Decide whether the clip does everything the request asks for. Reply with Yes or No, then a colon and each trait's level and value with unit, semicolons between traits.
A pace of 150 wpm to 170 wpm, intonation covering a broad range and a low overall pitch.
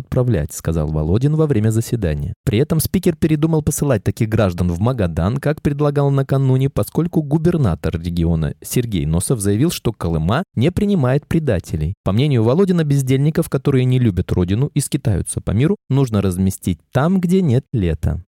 Yes: average, 155 wpm; wide, 7.9 semitones; low, 125 Hz